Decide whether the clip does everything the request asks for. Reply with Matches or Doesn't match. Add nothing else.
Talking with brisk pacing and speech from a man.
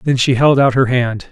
Matches